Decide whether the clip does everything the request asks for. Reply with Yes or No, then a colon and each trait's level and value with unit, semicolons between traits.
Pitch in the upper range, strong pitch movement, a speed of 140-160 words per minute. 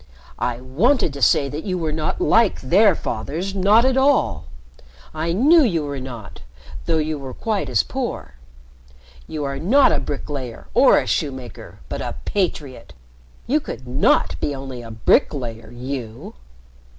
No: medium, 145 Hz; wide, 7.3 semitones; average, 155 wpm